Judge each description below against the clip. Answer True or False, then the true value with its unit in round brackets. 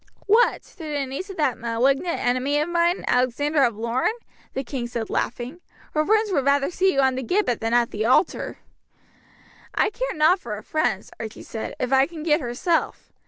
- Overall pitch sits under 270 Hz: False (275 Hz)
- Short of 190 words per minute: False (195 wpm)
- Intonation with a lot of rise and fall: True (5.8 semitones)